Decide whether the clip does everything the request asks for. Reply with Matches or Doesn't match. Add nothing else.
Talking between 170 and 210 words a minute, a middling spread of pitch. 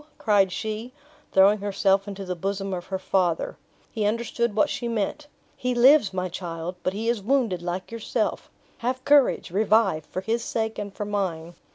Matches